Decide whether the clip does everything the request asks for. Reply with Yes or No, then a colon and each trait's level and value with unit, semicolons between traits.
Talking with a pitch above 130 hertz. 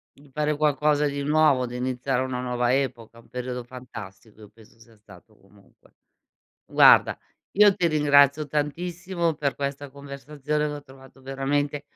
Yes: medium, 140 Hz